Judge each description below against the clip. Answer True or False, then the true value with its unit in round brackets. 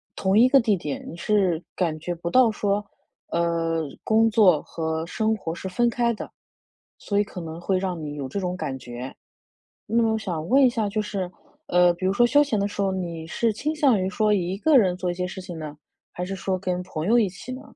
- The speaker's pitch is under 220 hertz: True (190 Hz)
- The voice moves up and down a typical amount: True (4.2 semitones)